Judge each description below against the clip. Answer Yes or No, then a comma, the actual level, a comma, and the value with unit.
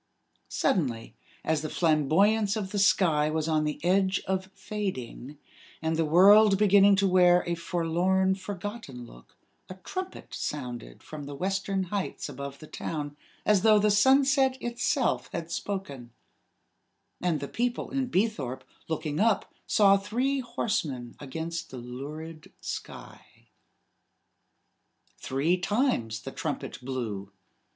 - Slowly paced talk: Yes, slow, 130 wpm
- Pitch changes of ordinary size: No, wide, 5.7 semitones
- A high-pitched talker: No, medium, 180 Hz